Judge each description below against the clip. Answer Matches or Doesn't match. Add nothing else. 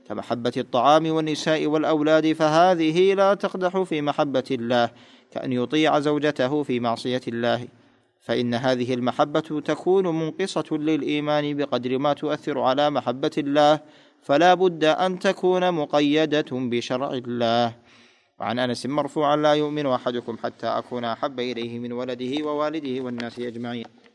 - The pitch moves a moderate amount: Matches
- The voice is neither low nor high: Matches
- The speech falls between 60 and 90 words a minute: Doesn't match